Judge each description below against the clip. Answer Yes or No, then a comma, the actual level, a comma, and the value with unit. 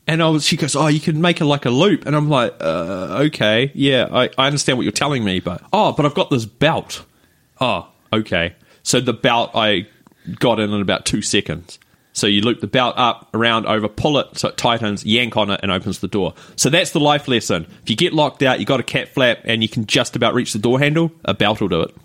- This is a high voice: No, low, 120 Hz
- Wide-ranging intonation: Yes, wide, 6.1 semitones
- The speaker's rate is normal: No, fast, 255 wpm